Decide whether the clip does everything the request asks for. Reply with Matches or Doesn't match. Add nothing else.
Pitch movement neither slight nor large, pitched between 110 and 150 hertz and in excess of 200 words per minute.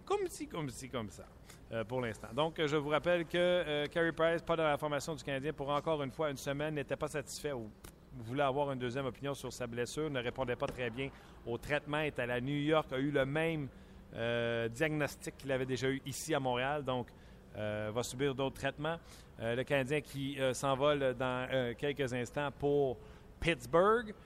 Matches